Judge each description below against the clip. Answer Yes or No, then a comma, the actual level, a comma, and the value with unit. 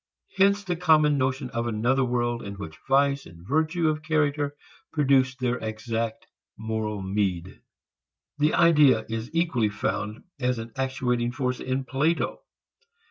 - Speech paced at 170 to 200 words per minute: No, slow, 135 wpm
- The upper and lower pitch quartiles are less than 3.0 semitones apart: No, average, 5.0 semitones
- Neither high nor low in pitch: No, low, 130 Hz